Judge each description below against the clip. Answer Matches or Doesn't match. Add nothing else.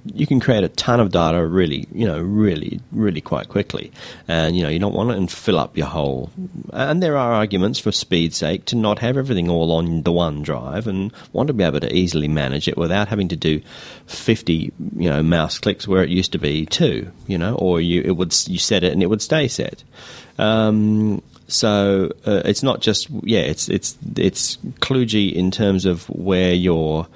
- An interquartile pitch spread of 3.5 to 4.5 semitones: Matches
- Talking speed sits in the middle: Doesn't match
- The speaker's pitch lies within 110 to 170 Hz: Doesn't match